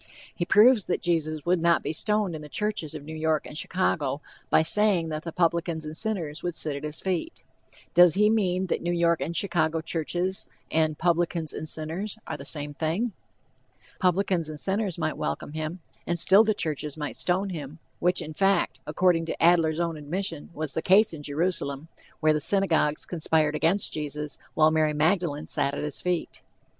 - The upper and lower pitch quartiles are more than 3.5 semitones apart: No, average, 2.9 semitones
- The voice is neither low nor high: Yes, medium, 165 Hz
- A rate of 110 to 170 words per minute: No, average, 190 wpm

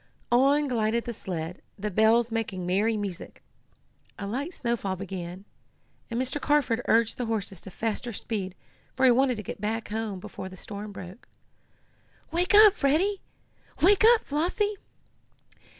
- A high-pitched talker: Yes, high, 225 Hz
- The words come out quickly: No, average, 150 wpm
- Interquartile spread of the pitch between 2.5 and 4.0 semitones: No, wide, 5.5 semitones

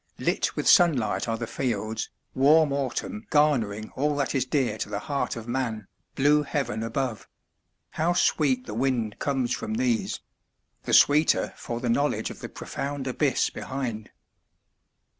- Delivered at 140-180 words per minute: Yes, average, 150 wpm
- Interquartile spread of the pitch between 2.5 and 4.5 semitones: Yes, average, 4.1 semitones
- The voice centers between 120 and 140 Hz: Yes, low, 135 Hz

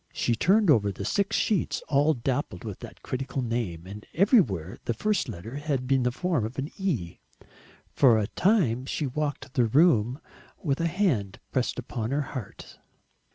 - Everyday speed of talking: Yes, average, 165 wpm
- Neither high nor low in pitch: No, low, 130 Hz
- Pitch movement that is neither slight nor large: No, wide, 5.7 semitones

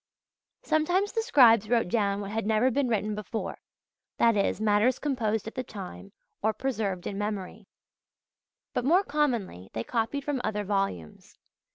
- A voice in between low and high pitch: No, high, 220 Hz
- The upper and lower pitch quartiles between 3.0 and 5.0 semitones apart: Yes, average, 4.2 semitones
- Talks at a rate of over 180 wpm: No, average, 155 wpm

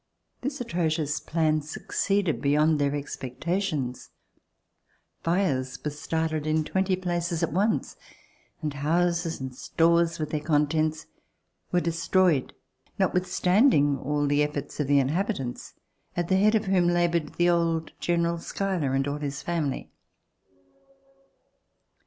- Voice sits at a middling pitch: Yes, medium, 165 Hz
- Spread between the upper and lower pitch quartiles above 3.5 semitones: No, average, 3.2 semitones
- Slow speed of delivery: Yes, slow, 120 wpm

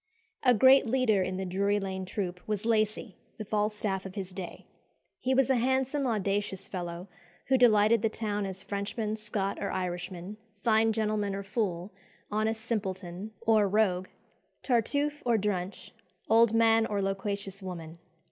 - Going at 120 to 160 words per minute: Yes, average, 150 wpm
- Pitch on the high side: Yes, high, 210 Hz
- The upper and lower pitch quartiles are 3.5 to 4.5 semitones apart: No, average, 2.7 semitones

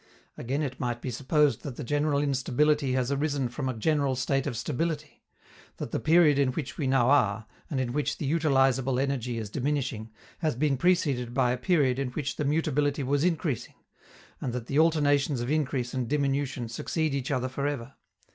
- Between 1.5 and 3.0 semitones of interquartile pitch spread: Yes, average, 2.7 semitones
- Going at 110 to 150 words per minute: No, average, 190 wpm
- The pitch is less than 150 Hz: Yes, medium, 140 Hz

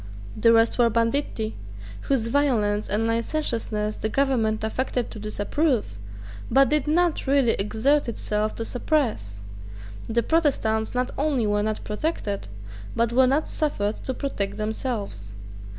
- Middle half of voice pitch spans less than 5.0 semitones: Yes, average, 4.4 semitones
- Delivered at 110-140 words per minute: Yes, slow, 135 wpm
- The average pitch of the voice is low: No, high, 230 Hz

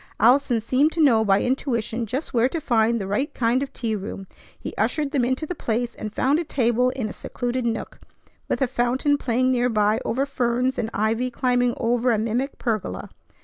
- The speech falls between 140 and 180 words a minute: No, average, 195 wpm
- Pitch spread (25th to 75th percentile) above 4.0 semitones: No, narrow, 2.6 semitones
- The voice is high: Yes, high, 245 Hz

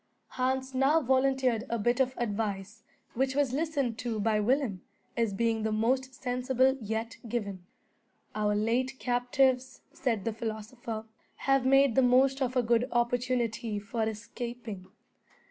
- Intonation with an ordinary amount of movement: Yes, average, 3.0 semitones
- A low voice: No, high, 240 Hz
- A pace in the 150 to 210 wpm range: No, average, 140 wpm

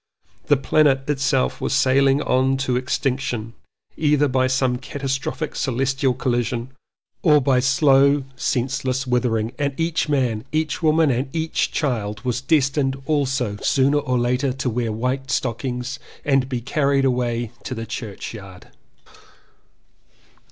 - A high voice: No, low, 130 Hz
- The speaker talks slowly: Yes, slow, 130 wpm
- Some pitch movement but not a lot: No, narrow, 2.0 semitones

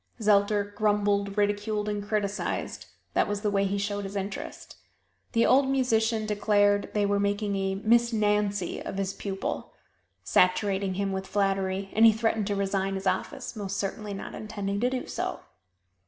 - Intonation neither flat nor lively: No, narrow, 1.2 semitones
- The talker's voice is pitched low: No, high, 205 Hz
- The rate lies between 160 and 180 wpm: Yes, average, 165 wpm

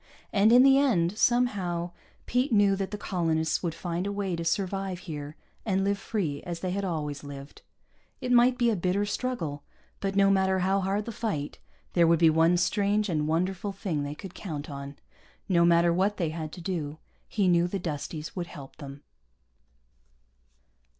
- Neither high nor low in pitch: Yes, medium, 180 Hz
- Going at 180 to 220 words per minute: Yes, average, 185 wpm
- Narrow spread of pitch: No, average, 3.7 semitones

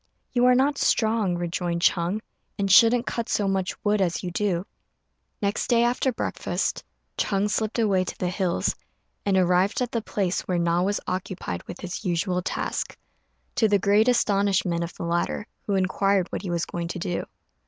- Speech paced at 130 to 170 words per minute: No, average, 180 wpm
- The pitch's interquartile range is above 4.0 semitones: No, average, 3.2 semitones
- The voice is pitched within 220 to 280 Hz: No, high, 195 Hz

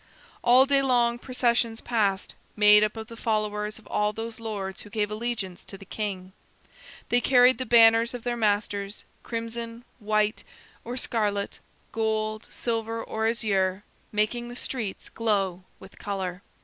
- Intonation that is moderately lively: No, narrow, 2.2 semitones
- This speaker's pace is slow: No, average, 150 wpm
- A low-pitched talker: No, high, 220 Hz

